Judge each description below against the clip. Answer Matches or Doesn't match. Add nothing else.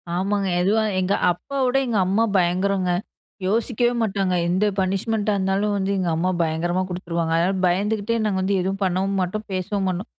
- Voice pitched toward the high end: Matches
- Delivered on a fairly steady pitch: Matches